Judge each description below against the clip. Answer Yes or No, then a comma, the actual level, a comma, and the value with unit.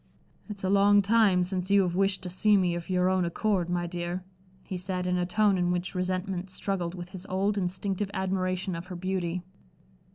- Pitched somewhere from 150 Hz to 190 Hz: Yes, medium, 185 Hz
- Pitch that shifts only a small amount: Yes, narrow, 1.6 semitones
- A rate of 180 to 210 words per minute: Yes, average, 200 wpm